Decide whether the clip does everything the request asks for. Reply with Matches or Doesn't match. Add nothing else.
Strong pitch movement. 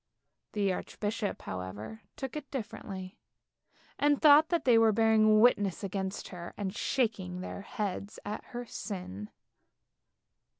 Doesn't match